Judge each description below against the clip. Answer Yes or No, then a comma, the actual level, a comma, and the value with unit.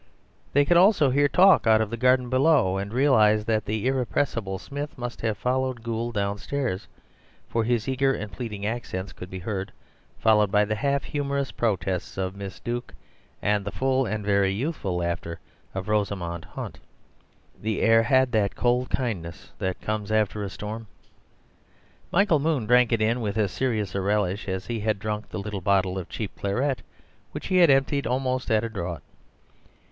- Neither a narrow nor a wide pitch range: Yes, average, 4.4 semitones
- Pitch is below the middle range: Yes, low, 110 Hz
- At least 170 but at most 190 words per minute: Yes, average, 175 wpm